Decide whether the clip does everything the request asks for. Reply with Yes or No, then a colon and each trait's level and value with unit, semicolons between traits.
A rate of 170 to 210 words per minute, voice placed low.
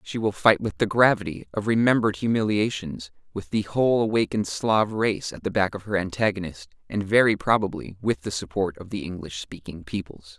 Yes: average, 185 wpm; low, 100 Hz